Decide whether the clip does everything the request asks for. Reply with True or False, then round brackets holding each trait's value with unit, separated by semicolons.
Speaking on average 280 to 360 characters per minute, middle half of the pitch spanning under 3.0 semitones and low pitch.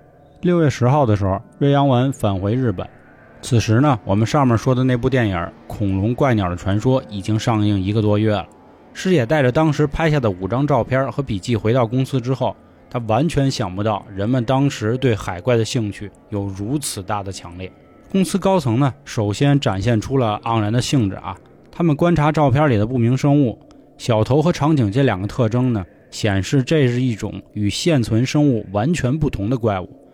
False (290 characters per minute; 5.2 semitones; 120 Hz)